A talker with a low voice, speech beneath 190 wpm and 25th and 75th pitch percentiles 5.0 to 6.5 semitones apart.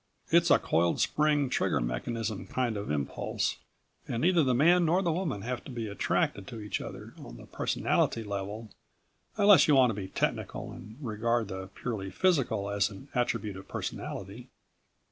Yes: low, 115 Hz; average, 170 wpm; average, 5.3 semitones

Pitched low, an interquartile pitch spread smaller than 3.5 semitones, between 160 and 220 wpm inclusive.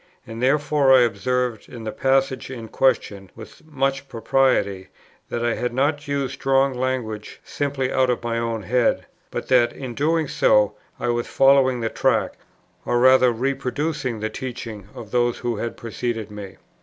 Yes: low, 125 Hz; average, 2.8 semitones; average, 165 wpm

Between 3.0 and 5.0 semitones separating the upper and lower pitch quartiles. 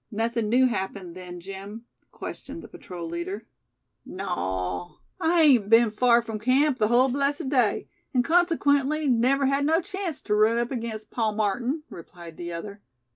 No: wide, 5.6 semitones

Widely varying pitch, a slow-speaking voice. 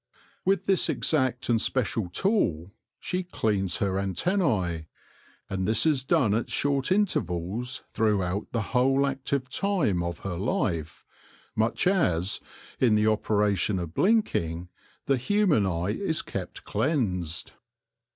Yes: wide, 7.3 semitones; slow, 125 wpm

